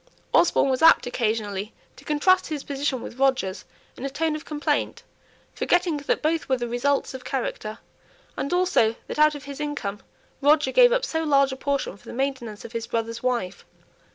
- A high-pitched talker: Yes, very high, 275 Hz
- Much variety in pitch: No, average, 4.4 semitones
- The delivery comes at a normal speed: Yes, average, 185 wpm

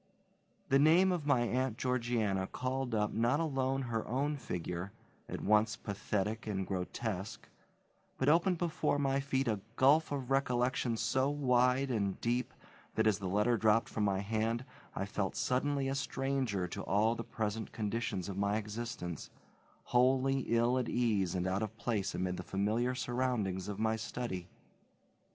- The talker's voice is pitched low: Yes, low, 115 Hz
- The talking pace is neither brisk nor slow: Yes, average, 160 wpm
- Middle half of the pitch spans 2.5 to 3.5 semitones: No, average, 4.2 semitones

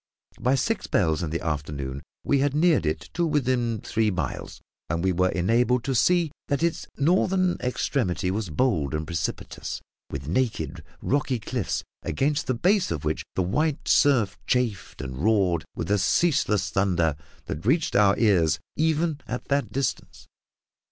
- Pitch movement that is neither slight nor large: No, wide, 8.8 semitones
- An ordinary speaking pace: Yes, average, 155 wpm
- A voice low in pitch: Yes, low, 110 Hz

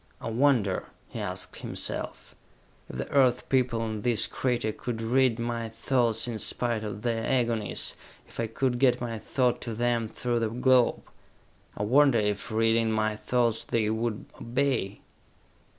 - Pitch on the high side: No, low, 115 Hz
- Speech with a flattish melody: Yes, narrow, 1.9 semitones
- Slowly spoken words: No, average, 155 wpm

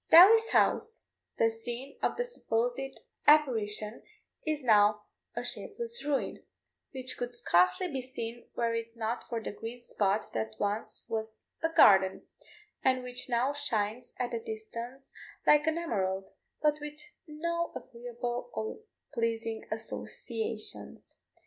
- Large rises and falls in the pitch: No, average, 4.7 semitones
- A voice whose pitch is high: Yes, high, 240 Hz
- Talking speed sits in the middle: No, slow, 130 wpm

